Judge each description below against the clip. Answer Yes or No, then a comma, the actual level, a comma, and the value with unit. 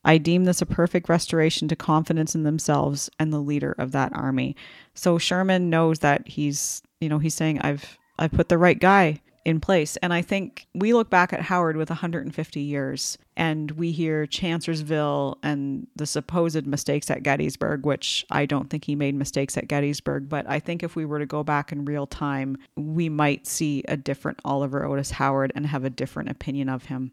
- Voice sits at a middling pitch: Yes, medium, 150 Hz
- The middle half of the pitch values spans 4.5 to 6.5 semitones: No, average, 2.8 semitones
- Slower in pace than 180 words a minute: No, average, 200 wpm